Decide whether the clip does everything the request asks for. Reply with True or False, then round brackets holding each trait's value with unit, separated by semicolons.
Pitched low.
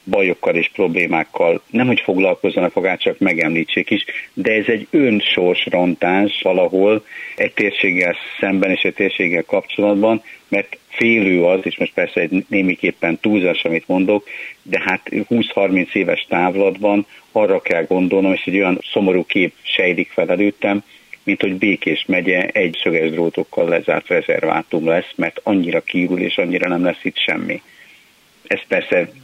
True (100 Hz)